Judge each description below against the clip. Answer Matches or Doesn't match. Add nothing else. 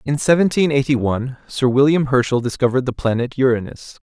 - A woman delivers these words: Doesn't match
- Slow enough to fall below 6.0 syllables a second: Doesn't match